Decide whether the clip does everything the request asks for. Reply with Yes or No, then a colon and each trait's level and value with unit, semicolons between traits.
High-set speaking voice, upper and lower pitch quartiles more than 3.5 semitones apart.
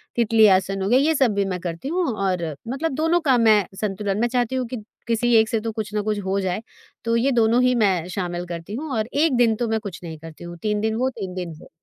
Yes: high, 220 Hz; average, 4.1 semitones